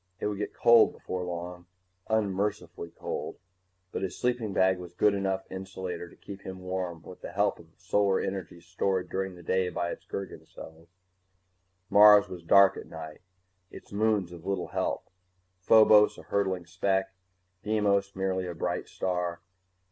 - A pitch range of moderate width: No, narrow, 2.1 semitones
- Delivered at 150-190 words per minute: Yes, average, 165 wpm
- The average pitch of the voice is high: No, very low, 95 Hz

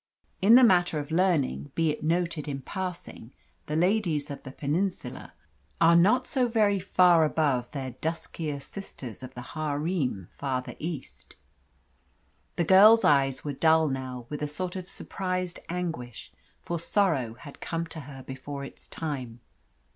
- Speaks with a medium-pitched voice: Yes, medium, 155 Hz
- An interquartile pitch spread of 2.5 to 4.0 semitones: No, average, 4.8 semitones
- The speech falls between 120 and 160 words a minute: Yes, average, 150 wpm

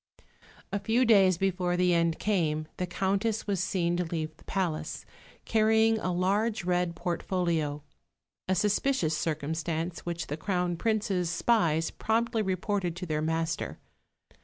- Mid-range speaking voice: Yes, medium, 180 Hz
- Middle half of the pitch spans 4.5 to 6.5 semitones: No, average, 3.7 semitones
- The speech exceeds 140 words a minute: No, slow, 135 wpm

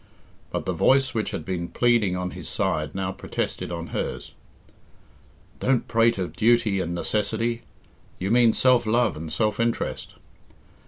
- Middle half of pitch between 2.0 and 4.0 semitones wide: No, average, 4.5 semitones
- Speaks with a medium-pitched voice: No, low, 110 Hz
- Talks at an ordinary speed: Yes, average, 150 wpm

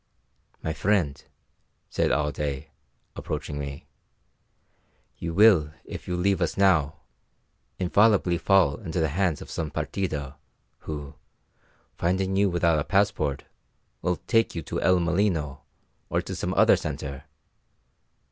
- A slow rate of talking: Yes, slow, 125 wpm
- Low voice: Yes, very low, 85 Hz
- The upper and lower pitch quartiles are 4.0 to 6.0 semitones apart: Yes, average, 4.5 semitones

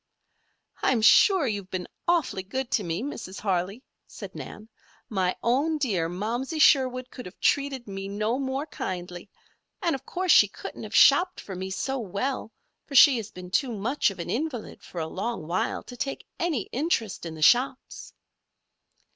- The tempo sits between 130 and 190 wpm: Yes, average, 170 wpm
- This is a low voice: No, high, 235 Hz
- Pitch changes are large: Yes, wide, 6.2 semitones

